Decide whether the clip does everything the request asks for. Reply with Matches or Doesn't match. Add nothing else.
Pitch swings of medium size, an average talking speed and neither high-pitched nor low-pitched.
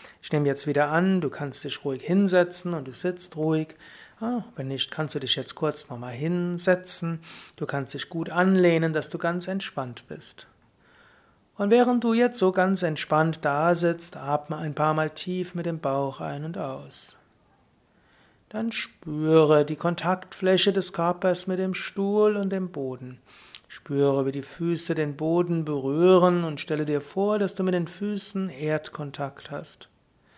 Matches